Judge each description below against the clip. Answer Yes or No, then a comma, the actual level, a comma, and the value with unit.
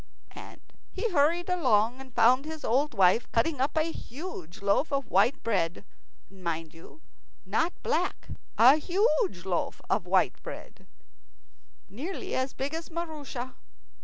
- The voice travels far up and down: Yes, wide, 7.2 semitones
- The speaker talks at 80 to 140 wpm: Yes, slow, 135 wpm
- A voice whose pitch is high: Yes, very high, 265 Hz